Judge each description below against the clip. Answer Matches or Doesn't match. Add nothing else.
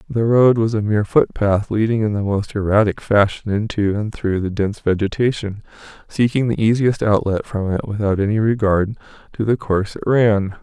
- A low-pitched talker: Matches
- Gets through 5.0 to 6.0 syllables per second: Matches